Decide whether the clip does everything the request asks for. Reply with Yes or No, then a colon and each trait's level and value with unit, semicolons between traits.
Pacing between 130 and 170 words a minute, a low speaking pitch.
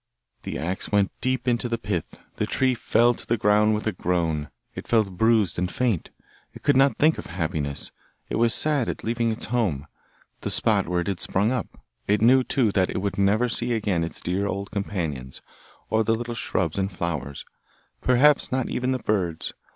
No: average, 195 wpm; low, 105 Hz